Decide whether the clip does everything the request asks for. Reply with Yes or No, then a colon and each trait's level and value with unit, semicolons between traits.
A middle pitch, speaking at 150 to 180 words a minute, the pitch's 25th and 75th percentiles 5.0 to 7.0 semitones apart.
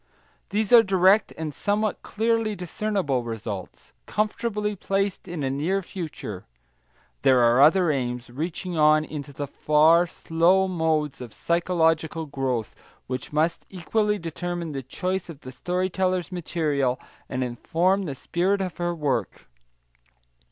No: medium, 165 Hz; slow, 135 wpm; average, 5.3 semitones